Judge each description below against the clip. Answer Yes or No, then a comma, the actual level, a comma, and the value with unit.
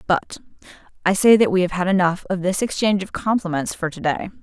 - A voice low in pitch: No, medium, 185 Hz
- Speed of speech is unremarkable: No, fast, 215 wpm